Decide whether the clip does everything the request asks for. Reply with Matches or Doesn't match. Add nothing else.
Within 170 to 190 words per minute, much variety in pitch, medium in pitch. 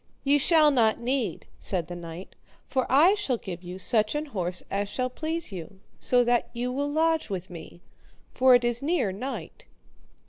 Doesn't match